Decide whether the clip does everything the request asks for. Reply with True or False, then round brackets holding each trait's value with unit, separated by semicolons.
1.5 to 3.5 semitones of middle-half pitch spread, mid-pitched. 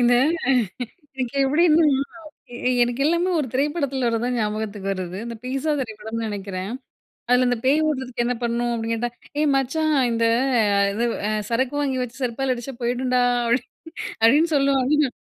False (3.0 semitones; 250 Hz)